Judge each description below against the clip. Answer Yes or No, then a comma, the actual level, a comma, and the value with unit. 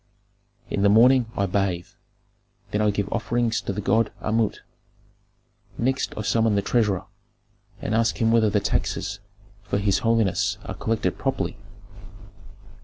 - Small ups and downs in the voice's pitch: Yes, narrow, 2.2 semitones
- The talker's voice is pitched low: Yes, low, 105 Hz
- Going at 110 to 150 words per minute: Yes, average, 140 wpm